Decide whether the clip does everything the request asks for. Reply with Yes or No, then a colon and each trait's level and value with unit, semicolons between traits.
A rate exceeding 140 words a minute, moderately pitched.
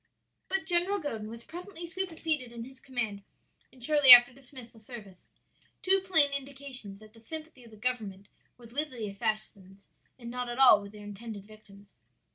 No: average, 175 wpm; high, 245 Hz